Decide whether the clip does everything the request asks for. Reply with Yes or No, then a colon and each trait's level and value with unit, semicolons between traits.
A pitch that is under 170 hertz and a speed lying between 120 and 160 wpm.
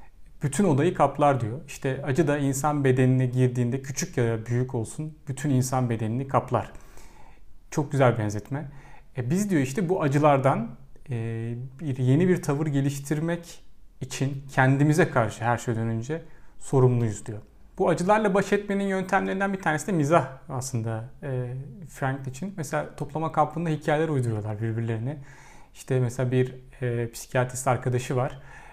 Yes: low, 135 Hz; fast, 140 wpm